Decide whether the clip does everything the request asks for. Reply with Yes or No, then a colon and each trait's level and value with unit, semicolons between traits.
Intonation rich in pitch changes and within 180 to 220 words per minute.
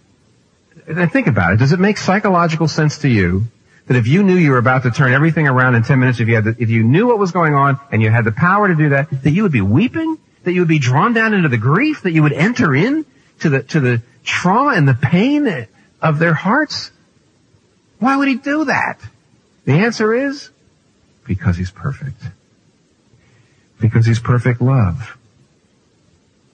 Yes: wide, 6.6 semitones; average, 200 wpm